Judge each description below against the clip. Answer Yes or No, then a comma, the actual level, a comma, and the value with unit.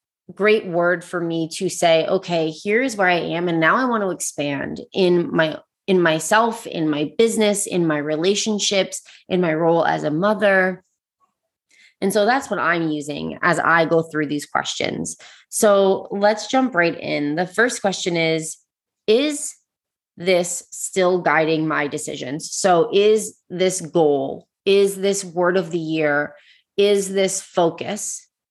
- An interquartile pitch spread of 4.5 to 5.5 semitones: No, average, 3.8 semitones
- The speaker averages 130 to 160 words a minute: Yes, average, 155 wpm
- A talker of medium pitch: Yes, medium, 180 Hz